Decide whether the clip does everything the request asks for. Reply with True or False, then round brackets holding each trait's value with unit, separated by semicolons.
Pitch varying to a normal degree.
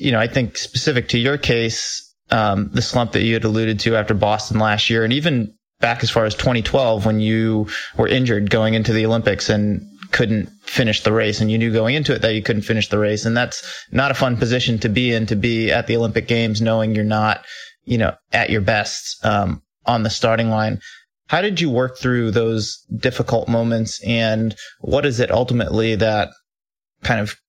False (1.7 semitones)